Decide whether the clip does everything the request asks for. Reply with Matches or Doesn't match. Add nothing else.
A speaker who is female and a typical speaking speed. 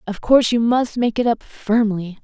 Doesn't match